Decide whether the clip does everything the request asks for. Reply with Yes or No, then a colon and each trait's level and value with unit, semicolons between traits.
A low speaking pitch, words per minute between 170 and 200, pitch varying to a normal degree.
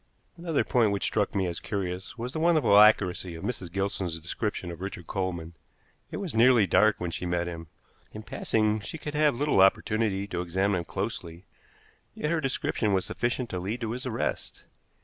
Yes: low, 100 Hz; average, 190 wpm; average, 5.0 semitones